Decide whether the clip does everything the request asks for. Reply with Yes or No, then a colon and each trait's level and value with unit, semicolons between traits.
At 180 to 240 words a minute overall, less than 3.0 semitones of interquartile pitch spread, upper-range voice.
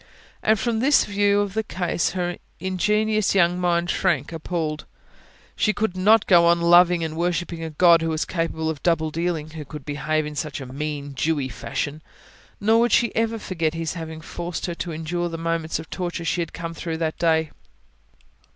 No: average, 190 wpm; narrow, 2.6 semitones; medium, 170 Hz